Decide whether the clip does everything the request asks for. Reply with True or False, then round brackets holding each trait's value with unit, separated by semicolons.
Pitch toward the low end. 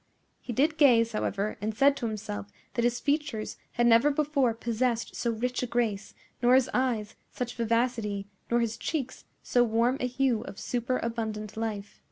False (235 Hz)